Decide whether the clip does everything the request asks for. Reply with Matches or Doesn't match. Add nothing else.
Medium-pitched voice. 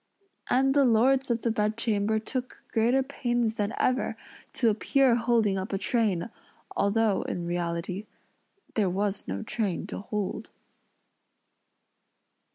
Doesn't match